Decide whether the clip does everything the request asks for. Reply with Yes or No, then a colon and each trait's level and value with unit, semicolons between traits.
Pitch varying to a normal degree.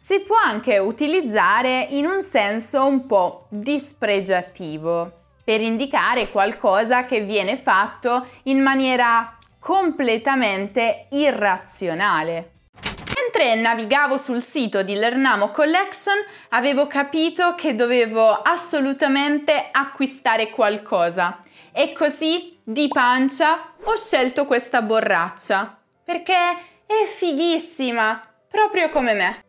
No: wide, 6.2 semitones